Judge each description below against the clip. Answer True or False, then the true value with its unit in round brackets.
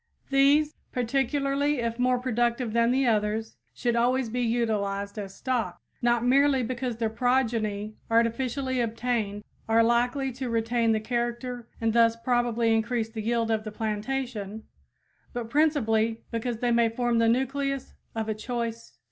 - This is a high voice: True (235 Hz)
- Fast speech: False (150 wpm)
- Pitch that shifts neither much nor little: False (2.1 semitones)